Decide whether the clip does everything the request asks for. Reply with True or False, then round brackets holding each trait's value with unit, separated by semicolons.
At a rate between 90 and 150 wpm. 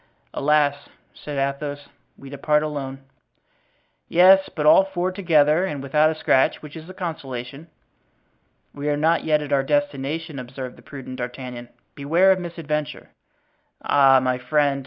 True (145 wpm)